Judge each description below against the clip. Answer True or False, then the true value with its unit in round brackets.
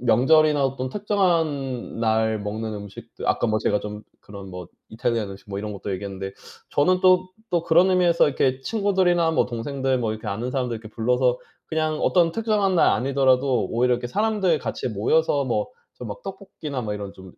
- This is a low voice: True (130 Hz)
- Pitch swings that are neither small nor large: False (7.2 semitones)